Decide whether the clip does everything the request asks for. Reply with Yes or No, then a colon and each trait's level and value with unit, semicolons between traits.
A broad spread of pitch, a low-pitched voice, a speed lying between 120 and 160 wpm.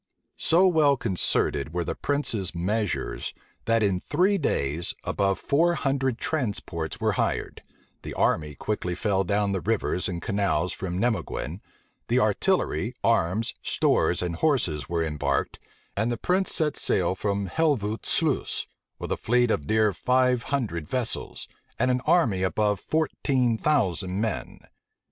Yes: wide, 6.2 semitones; low, 105 Hz; average, 145 wpm